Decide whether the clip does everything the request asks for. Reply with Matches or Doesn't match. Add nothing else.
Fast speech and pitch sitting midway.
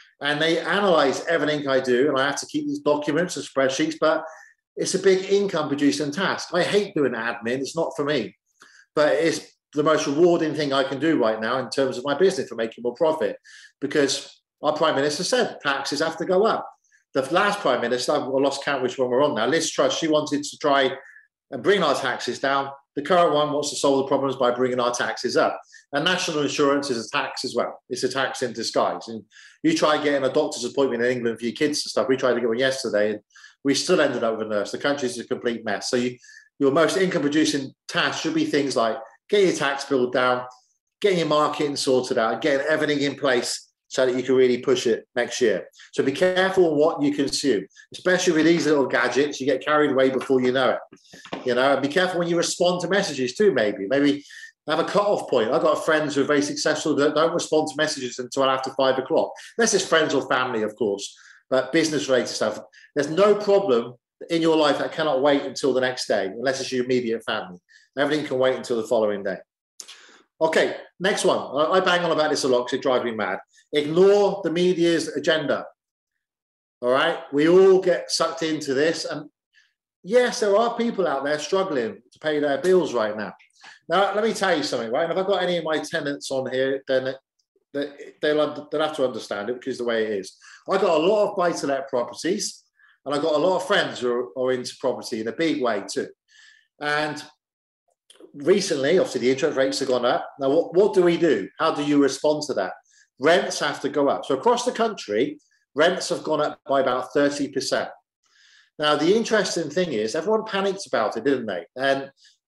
Matches